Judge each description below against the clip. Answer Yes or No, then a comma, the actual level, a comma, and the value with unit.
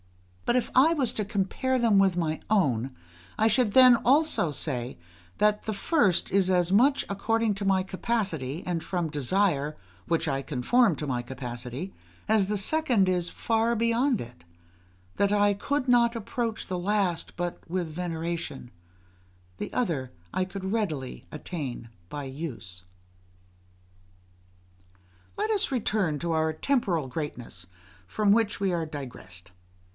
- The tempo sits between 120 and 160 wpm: Yes, average, 145 wpm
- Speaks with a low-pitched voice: No, medium, 185 Hz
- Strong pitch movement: Yes, wide, 6.7 semitones